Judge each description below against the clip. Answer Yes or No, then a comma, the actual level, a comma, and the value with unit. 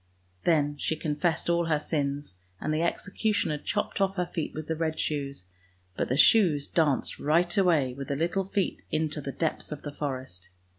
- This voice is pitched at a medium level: Yes, medium, 155 Hz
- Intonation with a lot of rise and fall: No, average, 3.2 semitones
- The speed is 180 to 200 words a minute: Yes, average, 190 wpm